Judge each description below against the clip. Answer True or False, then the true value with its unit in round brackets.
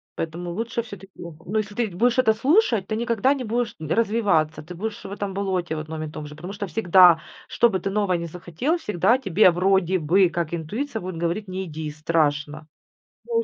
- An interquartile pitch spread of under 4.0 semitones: False (4.8 semitones)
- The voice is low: False (190 Hz)